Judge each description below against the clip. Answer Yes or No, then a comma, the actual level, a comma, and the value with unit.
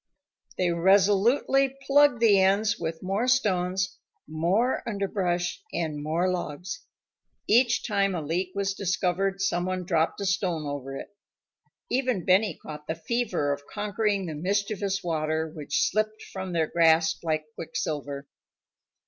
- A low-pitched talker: No, medium, 185 Hz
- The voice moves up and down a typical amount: Yes, average, 4.0 semitones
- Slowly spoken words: Yes, slow, 130 wpm